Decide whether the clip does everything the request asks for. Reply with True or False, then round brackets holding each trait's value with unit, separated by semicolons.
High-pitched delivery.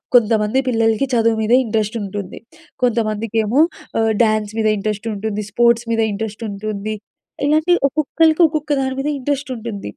True (225 Hz)